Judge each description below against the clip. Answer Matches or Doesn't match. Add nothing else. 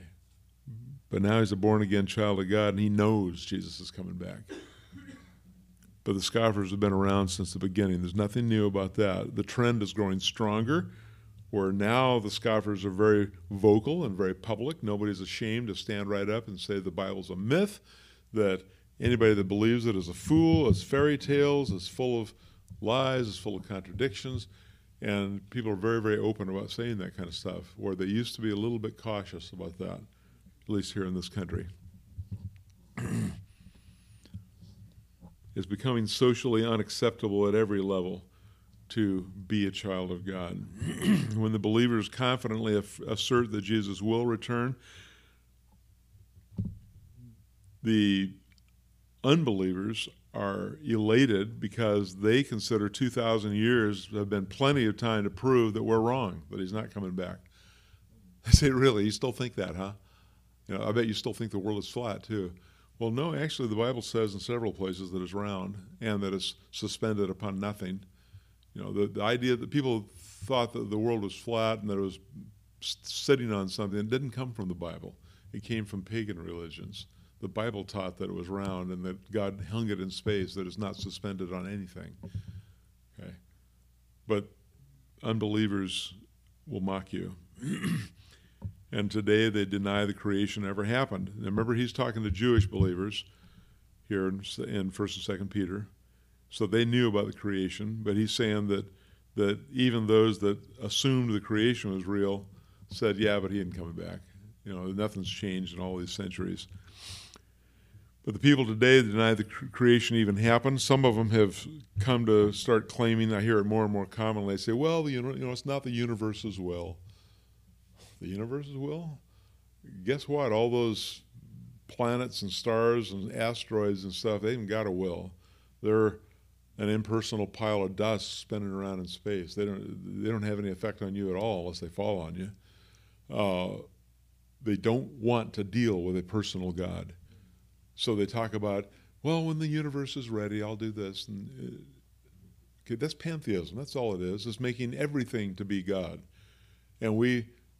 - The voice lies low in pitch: Matches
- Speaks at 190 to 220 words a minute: Doesn't match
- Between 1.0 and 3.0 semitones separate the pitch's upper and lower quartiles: Matches